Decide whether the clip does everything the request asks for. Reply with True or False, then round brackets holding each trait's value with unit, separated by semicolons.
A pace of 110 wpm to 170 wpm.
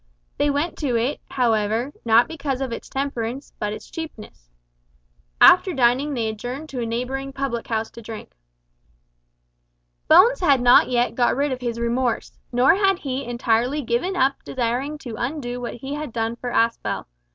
True (165 wpm)